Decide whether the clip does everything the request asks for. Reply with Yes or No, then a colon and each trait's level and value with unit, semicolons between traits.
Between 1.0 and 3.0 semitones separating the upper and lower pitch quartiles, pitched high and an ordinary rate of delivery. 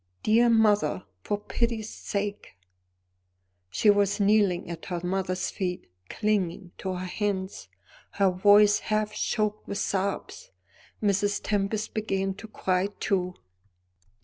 No: narrow, 2.5 semitones; high, 200 Hz; slow, 120 wpm